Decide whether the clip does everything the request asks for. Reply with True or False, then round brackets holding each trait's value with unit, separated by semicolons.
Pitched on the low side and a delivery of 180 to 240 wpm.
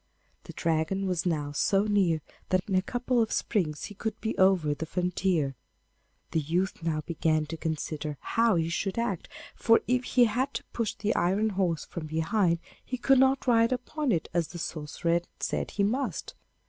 False (185 Hz; 185 wpm)